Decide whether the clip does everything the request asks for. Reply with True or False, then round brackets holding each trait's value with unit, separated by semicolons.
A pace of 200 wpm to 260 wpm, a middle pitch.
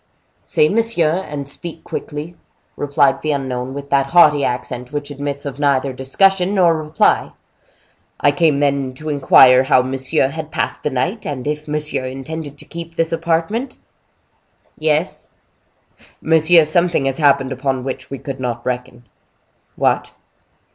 False (145 wpm; 145 Hz)